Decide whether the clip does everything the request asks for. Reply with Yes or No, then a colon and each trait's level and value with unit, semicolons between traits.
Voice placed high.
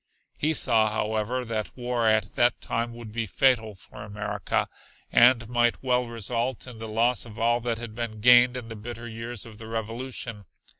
No: low, 115 Hz